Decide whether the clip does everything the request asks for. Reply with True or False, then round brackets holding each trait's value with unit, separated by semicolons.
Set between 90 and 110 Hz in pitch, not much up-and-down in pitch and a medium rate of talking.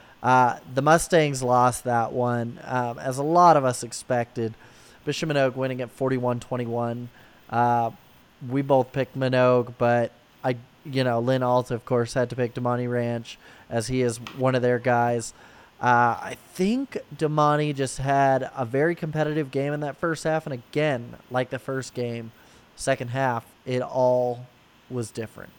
False (125 Hz; 2.1 semitones; 165 wpm)